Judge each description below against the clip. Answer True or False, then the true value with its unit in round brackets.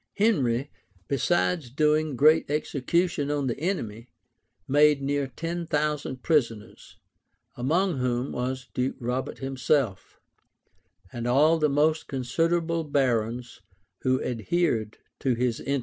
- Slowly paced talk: True (115 wpm)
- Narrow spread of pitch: False (4.0 semitones)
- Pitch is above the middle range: False (140 Hz)